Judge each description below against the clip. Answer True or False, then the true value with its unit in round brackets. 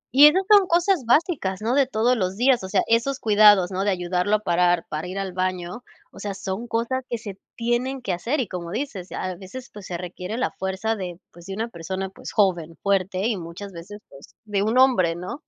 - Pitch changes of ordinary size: True (4.6 semitones)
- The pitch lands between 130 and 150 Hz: False (200 Hz)